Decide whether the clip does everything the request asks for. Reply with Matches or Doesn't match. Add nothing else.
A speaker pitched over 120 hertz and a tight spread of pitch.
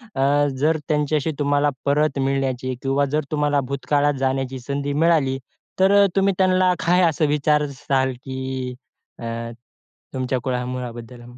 Matches